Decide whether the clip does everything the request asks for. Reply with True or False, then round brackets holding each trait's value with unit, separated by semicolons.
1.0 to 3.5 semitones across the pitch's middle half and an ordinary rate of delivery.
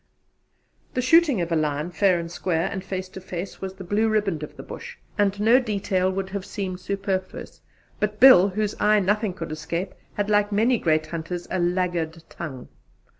True (3.2 semitones; 185 wpm)